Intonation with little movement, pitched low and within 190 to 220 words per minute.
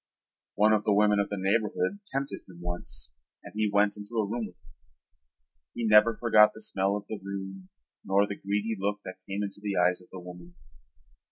Yes: narrow, 1.9 semitones; low, 100 Hz; average, 200 wpm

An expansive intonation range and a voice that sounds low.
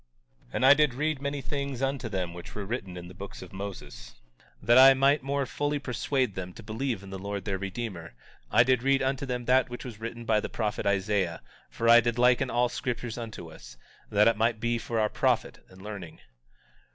No: average, 4.7 semitones; low, 115 Hz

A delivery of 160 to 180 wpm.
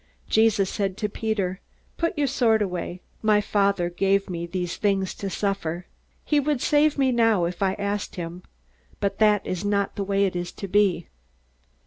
Yes: average, 175 wpm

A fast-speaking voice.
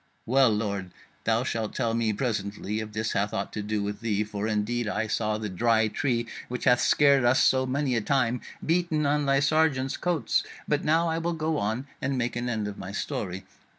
Yes: fast, 210 wpm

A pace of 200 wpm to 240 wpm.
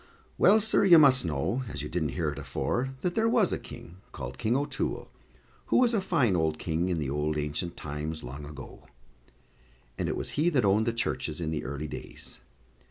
Yes: fast, 205 wpm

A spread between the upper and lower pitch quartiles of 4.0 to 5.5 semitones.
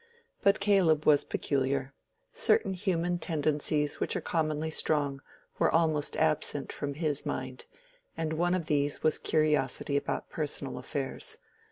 No: narrow, 2.4 semitones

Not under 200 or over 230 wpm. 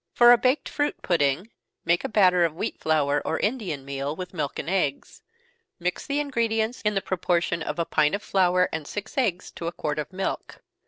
Yes: fast, 205 wpm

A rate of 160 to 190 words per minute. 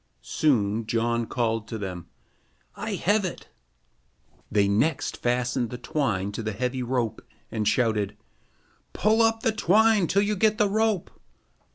No: average, 145 wpm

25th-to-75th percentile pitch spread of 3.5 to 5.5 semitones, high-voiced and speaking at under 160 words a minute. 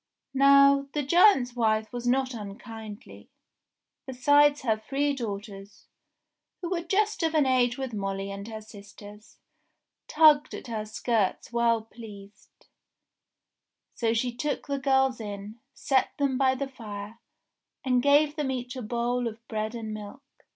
Yes: average, 4.2 semitones; high, 245 Hz; average, 145 wpm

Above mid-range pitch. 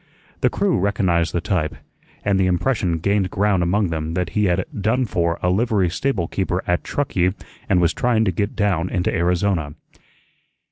No: very low, 95 Hz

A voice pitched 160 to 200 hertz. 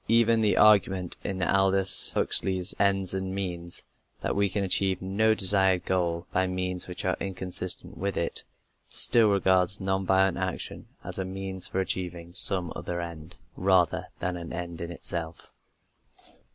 No: very low, 95 Hz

